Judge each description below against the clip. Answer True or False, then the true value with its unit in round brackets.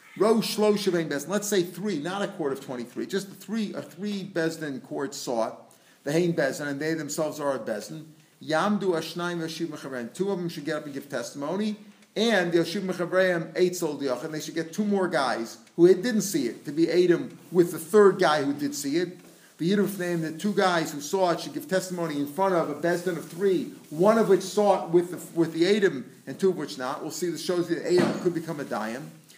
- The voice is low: False (175 Hz)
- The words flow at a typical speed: False (220 wpm)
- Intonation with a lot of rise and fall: False (3.7 semitones)